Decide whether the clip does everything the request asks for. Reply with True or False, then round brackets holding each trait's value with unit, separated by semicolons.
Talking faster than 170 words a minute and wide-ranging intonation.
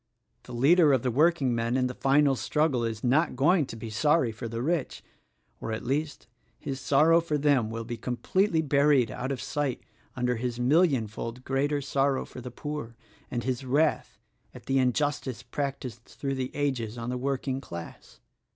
False (180 wpm; 3.3 semitones)